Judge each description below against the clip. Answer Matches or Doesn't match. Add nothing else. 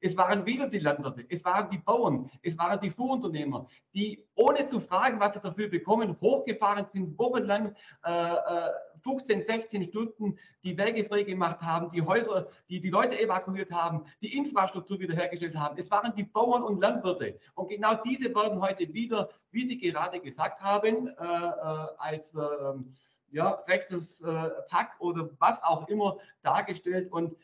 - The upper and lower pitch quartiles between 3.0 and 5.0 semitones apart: Matches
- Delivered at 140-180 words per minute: Matches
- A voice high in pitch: Matches